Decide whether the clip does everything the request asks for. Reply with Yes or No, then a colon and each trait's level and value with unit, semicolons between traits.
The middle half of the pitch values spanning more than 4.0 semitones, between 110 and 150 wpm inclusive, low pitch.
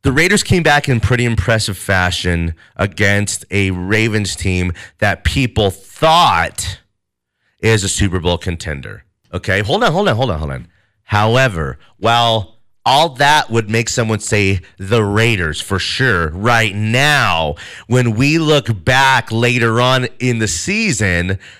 Yes: average, 4.5 semitones; average, 145 wpm; low, 110 Hz